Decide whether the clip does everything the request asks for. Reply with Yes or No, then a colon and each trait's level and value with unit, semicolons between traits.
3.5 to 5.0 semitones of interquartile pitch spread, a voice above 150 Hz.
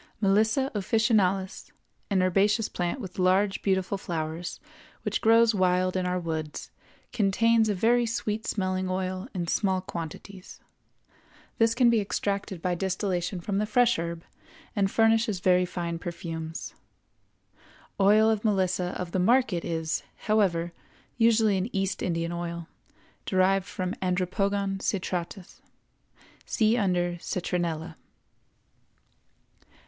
No: average, 3.1 semitones; high, 190 Hz